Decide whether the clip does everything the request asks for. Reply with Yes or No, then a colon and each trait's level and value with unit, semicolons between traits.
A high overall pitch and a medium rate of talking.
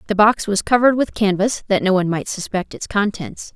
No: high, 200 Hz; fast, 220 wpm